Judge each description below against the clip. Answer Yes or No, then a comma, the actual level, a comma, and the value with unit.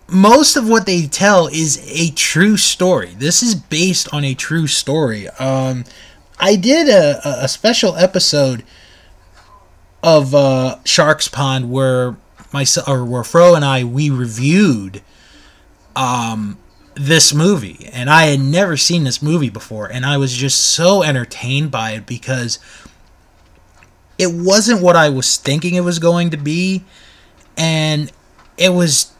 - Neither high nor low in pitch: Yes, medium, 145 Hz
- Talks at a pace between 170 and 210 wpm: No, average, 145 wpm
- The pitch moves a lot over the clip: Yes, wide, 6.0 semitones